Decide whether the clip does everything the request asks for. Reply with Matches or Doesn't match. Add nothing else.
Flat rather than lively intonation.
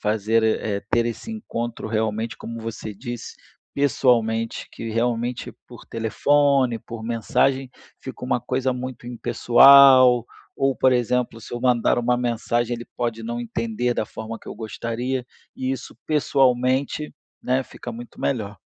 Matches